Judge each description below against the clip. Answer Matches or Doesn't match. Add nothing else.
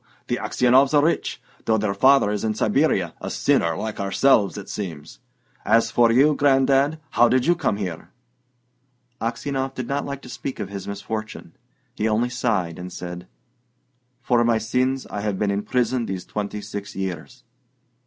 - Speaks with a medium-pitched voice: Doesn't match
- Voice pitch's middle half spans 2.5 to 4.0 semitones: Doesn't match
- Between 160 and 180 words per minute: Matches